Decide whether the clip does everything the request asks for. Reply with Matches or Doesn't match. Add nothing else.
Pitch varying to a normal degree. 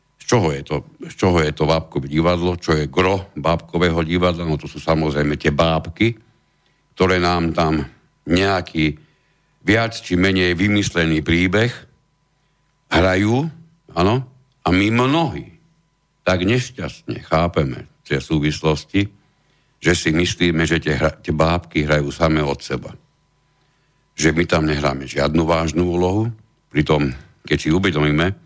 Matches